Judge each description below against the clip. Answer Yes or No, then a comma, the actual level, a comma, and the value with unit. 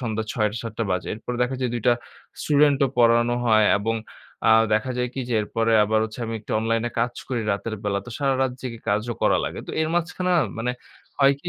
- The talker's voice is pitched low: Yes, low, 115 Hz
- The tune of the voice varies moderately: Yes, average, 3.0 semitones